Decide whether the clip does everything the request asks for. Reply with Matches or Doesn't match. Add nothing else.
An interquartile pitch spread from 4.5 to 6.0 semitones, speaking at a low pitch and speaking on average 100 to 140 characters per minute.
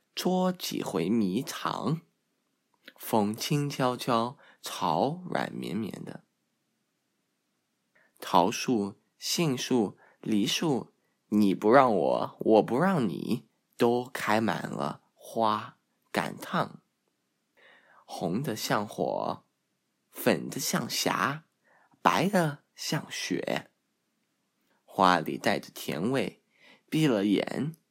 Matches